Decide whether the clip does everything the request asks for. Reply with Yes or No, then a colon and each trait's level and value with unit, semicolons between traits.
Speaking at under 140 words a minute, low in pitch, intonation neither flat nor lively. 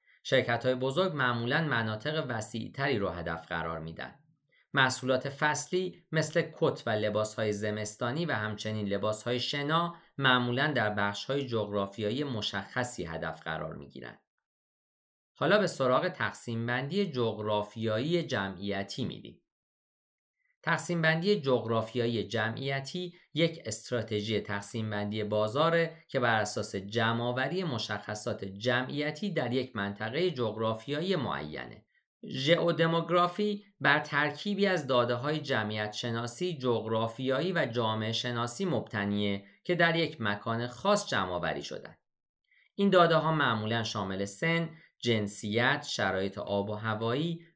No: average, 115 wpm; low, 120 Hz; wide, 6.7 semitones